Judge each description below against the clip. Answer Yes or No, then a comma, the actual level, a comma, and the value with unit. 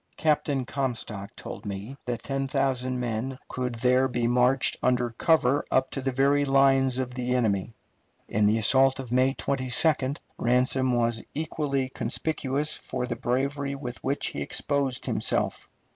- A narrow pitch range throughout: Yes, narrow, 1.9 semitones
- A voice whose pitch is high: No, low, 130 Hz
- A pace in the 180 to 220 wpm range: No, average, 150 wpm